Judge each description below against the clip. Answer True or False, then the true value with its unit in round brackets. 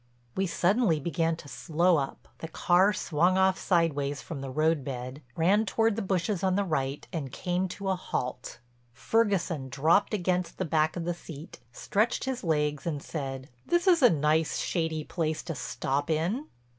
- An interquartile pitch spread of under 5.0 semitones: True (4.2 semitones)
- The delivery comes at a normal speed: True (170 wpm)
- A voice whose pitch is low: False (165 Hz)